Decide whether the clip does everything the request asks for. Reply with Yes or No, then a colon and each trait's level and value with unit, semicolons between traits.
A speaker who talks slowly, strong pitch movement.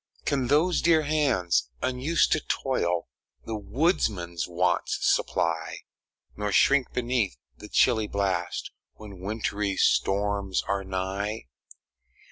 Yes: slow, 105 wpm; wide, 5.8 semitones